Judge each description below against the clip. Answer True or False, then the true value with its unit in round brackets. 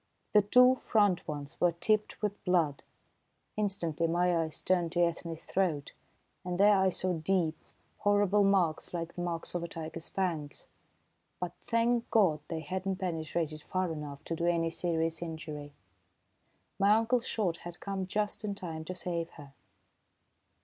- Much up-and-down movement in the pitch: False (3.2 semitones)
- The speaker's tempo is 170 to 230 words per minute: False (155 wpm)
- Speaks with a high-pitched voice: False (175 Hz)